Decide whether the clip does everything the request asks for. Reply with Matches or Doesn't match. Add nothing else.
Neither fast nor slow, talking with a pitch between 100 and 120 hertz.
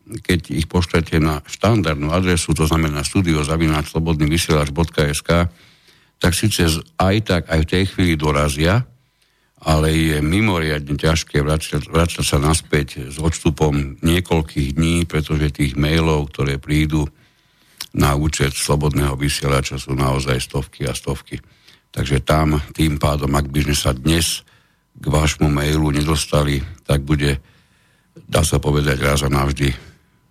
Doesn't match